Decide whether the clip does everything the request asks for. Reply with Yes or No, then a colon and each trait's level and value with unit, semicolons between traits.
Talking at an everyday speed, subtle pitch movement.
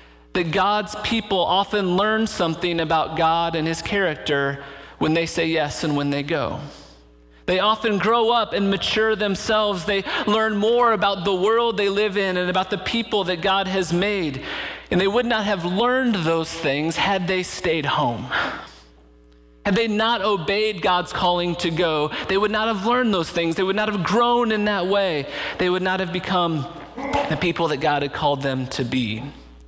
No: average, 185 wpm; average, 4.9 semitones